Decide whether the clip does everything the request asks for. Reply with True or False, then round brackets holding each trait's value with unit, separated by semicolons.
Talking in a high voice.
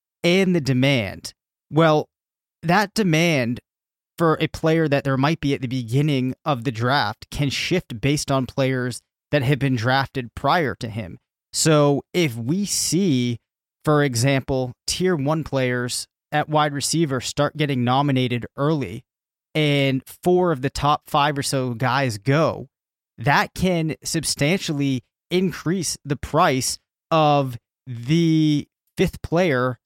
False (140 Hz)